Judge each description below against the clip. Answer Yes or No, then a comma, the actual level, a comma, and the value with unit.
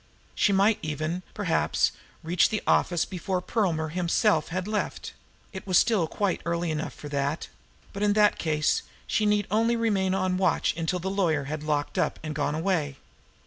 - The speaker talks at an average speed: Yes, average, 175 wpm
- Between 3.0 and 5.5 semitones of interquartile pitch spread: Yes, average, 4.3 semitones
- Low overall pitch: No, medium, 180 Hz